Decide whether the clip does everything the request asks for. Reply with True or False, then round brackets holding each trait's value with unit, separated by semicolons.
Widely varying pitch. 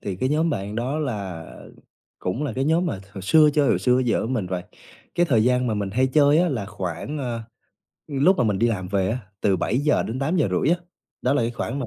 True (6.2 semitones)